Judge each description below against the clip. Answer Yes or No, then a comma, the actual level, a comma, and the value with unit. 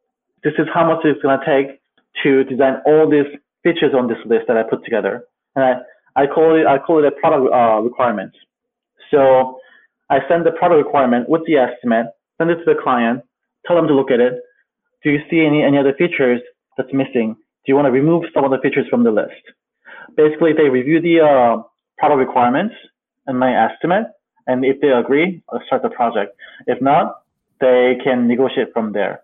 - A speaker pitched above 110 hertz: Yes, medium, 140 Hz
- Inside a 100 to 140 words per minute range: No, average, 200 wpm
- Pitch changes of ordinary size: Yes, average, 3.9 semitones